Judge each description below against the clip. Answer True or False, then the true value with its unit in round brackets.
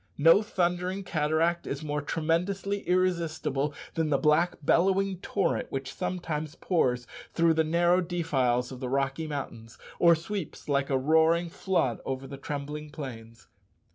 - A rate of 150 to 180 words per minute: False (140 wpm)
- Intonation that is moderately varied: True (4.1 semitones)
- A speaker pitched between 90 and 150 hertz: False (160 Hz)